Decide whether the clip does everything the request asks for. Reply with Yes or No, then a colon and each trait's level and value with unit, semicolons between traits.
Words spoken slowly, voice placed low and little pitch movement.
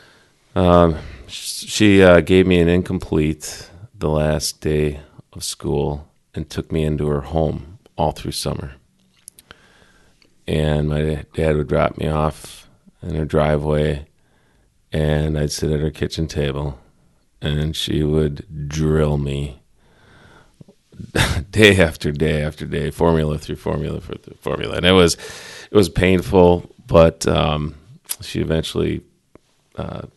Yes: slow, 125 wpm; very low, 75 Hz; narrow, 1.7 semitones